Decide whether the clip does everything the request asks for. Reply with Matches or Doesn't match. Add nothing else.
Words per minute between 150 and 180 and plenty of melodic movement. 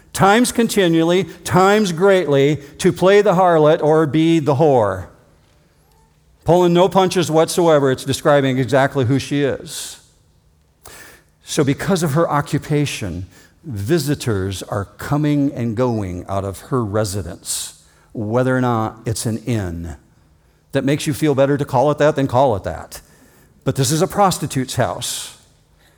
Doesn't match